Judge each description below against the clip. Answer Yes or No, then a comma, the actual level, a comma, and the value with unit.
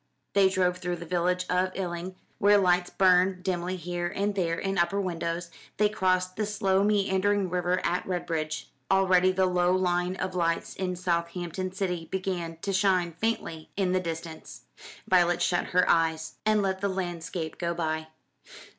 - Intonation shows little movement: Yes, narrow, 1.6 semitones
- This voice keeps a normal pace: Yes, average, 165 wpm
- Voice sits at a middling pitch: Yes, medium, 180 Hz